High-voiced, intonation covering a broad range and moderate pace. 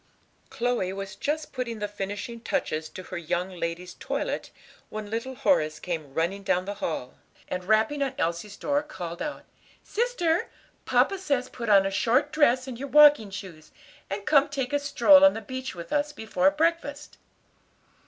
Yes: high, 230 Hz; wide, 7.2 semitones; average, 170 wpm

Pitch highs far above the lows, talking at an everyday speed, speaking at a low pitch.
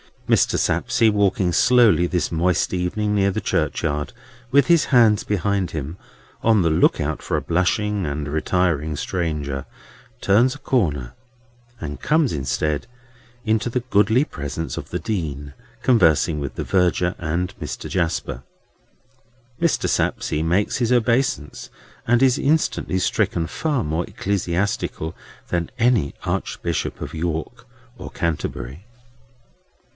No: wide, 6.1 semitones; slow, 130 wpm; very low, 90 Hz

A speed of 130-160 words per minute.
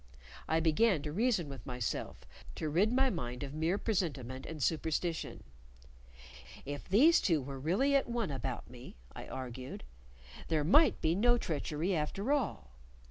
Yes: average, 150 wpm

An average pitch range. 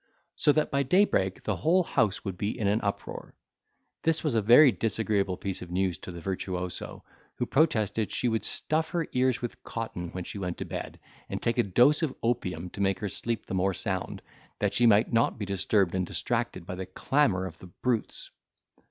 Yes: average, 4.8 semitones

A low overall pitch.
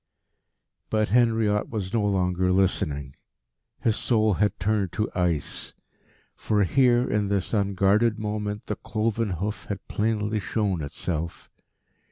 Yes: low, 105 Hz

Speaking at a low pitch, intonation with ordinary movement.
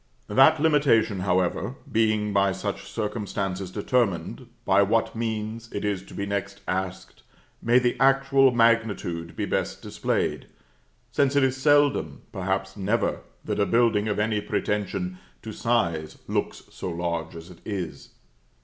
Yes: low, 105 Hz; average, 3.8 semitones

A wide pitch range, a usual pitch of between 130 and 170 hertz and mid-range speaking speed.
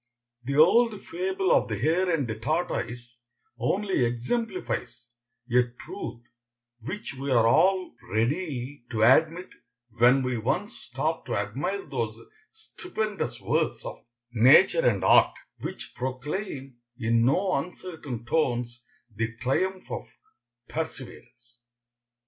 No: wide, 7.7 semitones; low, 135 Hz; slow, 115 wpm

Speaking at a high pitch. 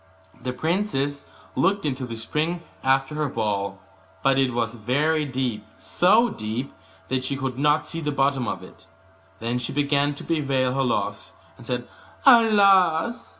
No: low, 135 Hz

